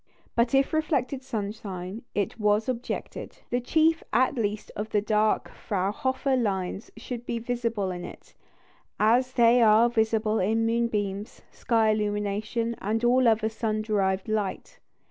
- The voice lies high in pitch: Yes, high, 220 Hz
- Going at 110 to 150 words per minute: Yes, average, 140 wpm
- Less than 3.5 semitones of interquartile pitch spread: Yes, narrow, 2.5 semitones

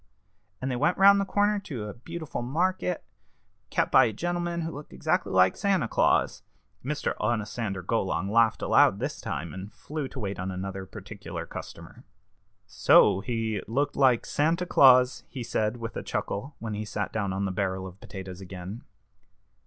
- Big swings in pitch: Yes, wide, 7.3 semitones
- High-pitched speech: No, low, 115 Hz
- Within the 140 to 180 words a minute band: Yes, average, 175 wpm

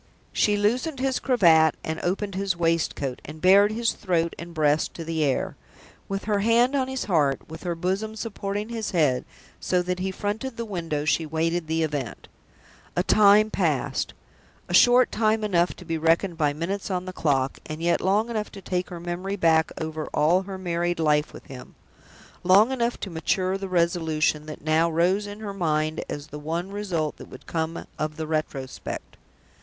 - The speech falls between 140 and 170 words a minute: No, average, 185 wpm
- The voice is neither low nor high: Yes, medium, 175 Hz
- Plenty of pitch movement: No, average, 4.2 semitones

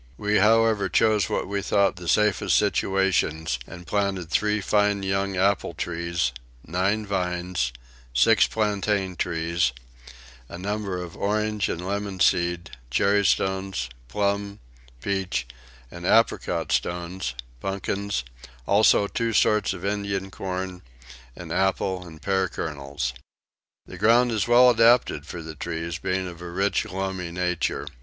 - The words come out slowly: Yes, slow, 130 wpm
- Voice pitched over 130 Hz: No, very low, 95 Hz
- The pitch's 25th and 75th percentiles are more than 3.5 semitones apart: No, average, 2.8 semitones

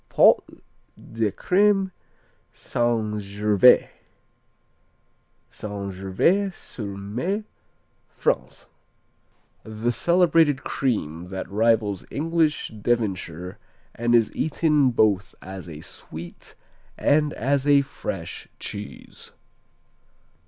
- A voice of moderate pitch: No, low, 115 Hz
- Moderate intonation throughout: No, wide, 6.6 semitones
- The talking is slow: Yes, slow, 85 wpm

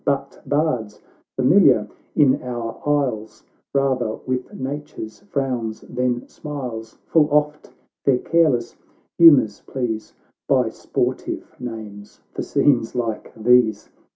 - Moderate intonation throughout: Yes, average, 4.1 semitones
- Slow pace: Yes, slow, 105 wpm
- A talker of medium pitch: No, low, 125 Hz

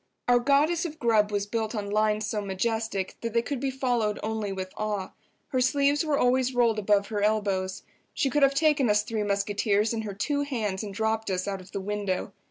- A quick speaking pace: Yes, fast, 210 wpm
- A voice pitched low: No, high, 215 Hz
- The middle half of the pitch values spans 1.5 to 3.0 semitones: No, average, 3.7 semitones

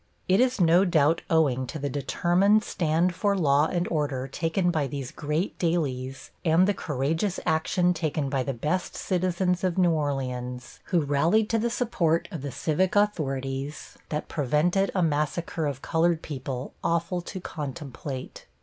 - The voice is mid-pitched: Yes, medium, 160 Hz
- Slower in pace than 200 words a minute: Yes, average, 160 wpm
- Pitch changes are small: No, average, 4.2 semitones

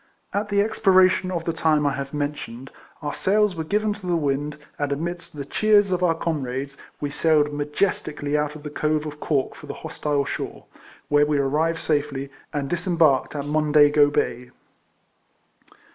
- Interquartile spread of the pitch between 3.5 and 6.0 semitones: No, average, 3.1 semitones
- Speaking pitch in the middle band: Yes, medium, 150 Hz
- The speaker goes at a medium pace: Yes, average, 170 wpm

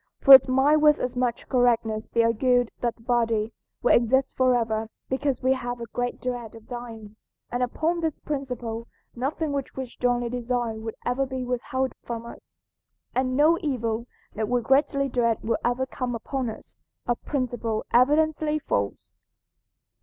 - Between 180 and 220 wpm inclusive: No, average, 160 wpm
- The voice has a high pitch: Yes, high, 245 Hz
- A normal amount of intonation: No, narrow, 2.3 semitones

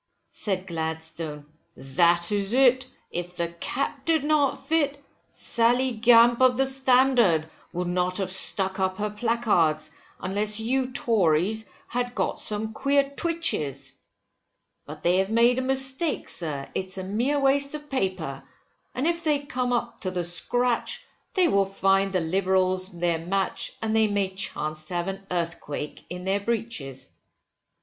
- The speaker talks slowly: No, average, 150 wpm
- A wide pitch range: Yes, wide, 6.1 semitones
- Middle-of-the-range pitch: No, high, 200 Hz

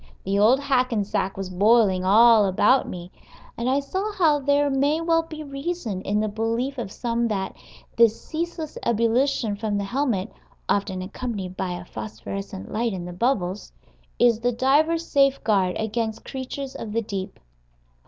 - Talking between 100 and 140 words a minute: No, average, 155 wpm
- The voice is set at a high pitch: Yes, high, 230 Hz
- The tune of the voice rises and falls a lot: Yes, wide, 5.8 semitones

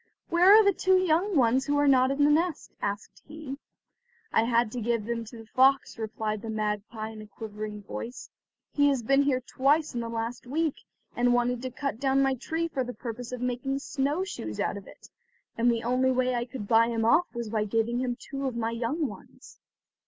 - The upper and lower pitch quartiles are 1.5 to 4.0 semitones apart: Yes, average, 3.4 semitones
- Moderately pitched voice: No, high, 245 Hz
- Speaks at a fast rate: Yes, fast, 220 wpm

